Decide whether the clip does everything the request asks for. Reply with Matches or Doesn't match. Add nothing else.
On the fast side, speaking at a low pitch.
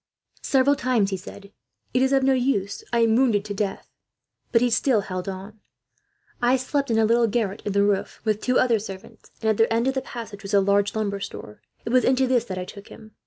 Doesn't match